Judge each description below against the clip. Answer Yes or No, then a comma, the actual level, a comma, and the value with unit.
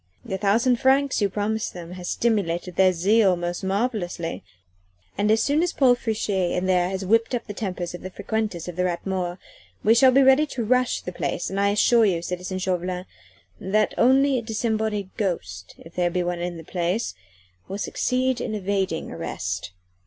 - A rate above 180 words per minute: Yes, average, 190 wpm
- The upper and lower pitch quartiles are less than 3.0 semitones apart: No, average, 4.2 semitones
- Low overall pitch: No, high, 195 Hz